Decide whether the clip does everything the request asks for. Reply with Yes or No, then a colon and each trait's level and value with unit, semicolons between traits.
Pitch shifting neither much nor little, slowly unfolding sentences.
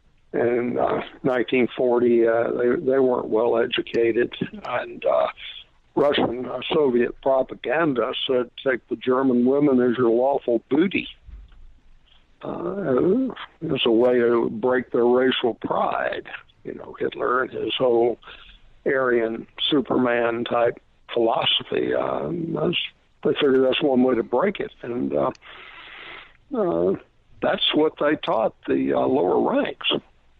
No: narrow, 1.8 semitones; slow, 125 wpm